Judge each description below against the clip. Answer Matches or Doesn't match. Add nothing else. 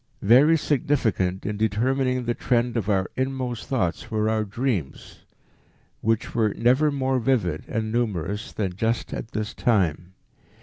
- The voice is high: Doesn't match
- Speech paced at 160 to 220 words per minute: Doesn't match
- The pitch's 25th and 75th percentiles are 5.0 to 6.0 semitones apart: Doesn't match